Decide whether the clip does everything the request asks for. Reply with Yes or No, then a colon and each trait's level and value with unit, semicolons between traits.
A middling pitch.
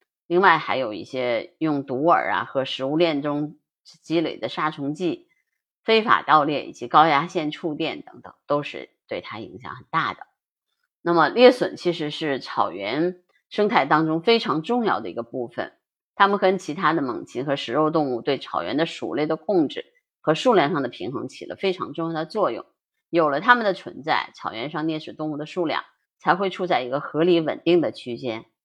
Yes: medium, 160 Hz